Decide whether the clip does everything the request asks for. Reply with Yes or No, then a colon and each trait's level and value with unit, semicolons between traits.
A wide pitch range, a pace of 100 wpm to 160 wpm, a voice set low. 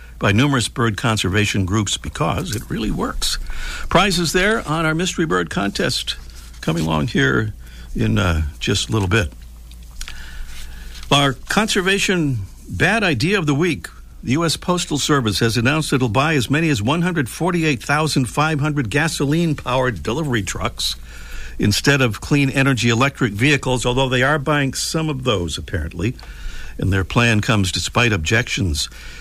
Yes: wide, 8.8 semitones; average, 140 wpm; low, 120 Hz